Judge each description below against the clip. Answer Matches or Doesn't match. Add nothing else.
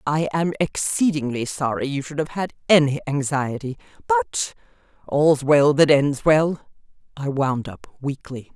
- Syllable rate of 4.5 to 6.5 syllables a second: Doesn't match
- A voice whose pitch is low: Doesn't match